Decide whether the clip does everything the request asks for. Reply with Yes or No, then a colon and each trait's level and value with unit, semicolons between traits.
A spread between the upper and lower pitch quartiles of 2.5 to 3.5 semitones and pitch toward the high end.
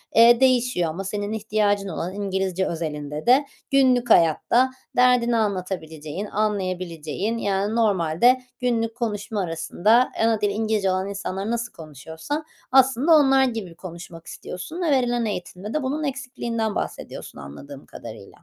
No: average, 5.0 semitones; high, 210 Hz